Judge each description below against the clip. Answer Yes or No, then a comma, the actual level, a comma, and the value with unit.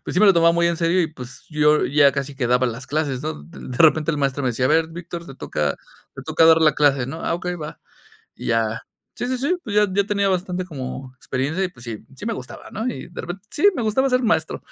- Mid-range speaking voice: Yes, medium, 155 Hz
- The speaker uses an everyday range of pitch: No, wide, 5.7 semitones